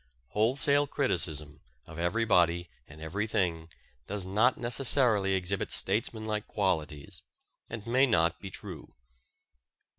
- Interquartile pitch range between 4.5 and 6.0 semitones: Yes, average, 5.3 semitones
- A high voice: No, low, 100 Hz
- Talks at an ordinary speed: No, slow, 100 wpm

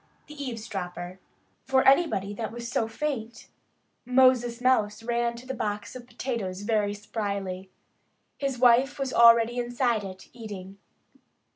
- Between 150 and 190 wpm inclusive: No, slow, 135 wpm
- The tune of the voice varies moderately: Yes, average, 3.5 semitones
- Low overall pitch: No, high, 235 Hz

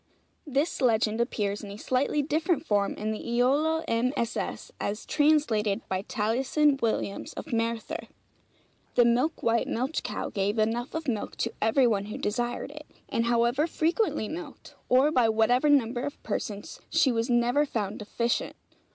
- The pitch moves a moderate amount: Yes, average, 4.7 semitones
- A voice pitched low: No, high, 240 Hz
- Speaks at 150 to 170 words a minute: Yes, average, 155 wpm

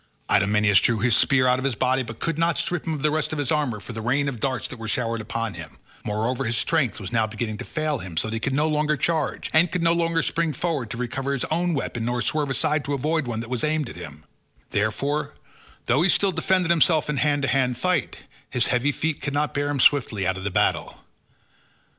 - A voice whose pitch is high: No, low, 135 Hz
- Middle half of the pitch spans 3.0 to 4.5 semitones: No, average, 5.0 semitones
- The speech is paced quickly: Yes, fast, 245 wpm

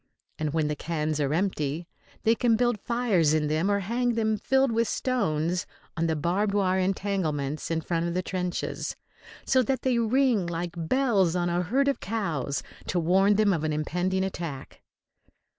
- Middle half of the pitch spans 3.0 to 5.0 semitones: No, wide, 5.5 semitones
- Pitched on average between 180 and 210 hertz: Yes, medium, 185 Hz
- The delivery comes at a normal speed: Yes, average, 175 wpm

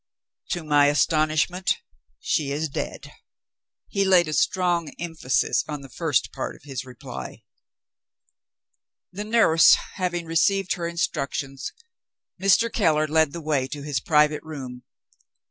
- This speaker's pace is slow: Yes, slow, 130 wpm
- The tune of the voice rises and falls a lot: No, average, 3.2 semitones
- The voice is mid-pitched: Yes, medium, 155 Hz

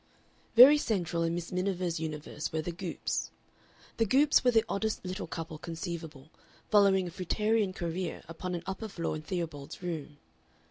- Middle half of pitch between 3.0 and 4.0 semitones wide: Yes, average, 3.3 semitones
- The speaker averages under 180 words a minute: Yes, average, 155 wpm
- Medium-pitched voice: Yes, medium, 175 Hz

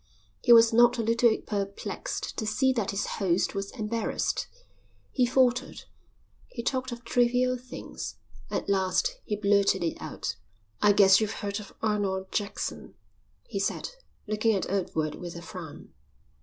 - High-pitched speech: Yes, high, 215 Hz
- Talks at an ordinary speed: Yes, average, 150 wpm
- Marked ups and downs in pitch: No, average, 3.4 semitones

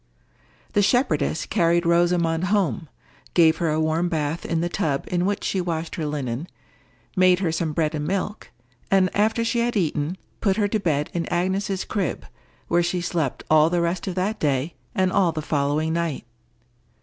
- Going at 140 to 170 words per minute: No, average, 185 wpm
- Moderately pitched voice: Yes, medium, 170 Hz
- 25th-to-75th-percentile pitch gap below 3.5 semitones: Yes, average, 3.1 semitones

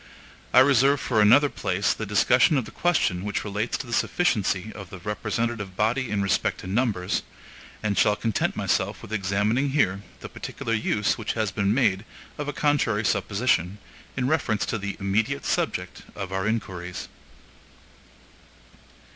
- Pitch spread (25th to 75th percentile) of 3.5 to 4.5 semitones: Yes, average, 4.0 semitones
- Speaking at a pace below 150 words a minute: No, average, 155 wpm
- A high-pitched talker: No, low, 105 Hz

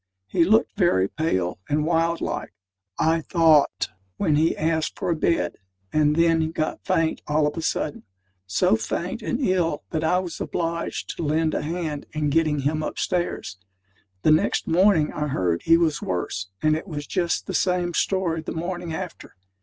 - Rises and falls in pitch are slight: Yes, narrow, 2.3 semitones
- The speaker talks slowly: No, average, 175 wpm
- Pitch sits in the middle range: Yes, medium, 160 Hz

